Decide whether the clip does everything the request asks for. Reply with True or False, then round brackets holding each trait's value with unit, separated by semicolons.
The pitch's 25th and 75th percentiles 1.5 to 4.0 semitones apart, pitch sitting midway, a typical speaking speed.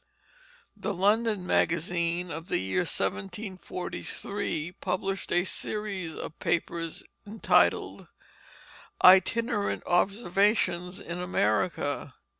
False (3.1 semitones; 180 Hz; 80 wpm)